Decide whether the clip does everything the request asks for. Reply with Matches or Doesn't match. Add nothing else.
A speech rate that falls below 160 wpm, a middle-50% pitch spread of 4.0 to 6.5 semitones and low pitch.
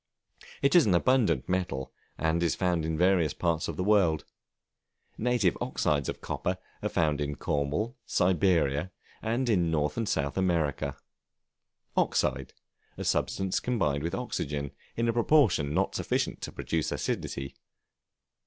Matches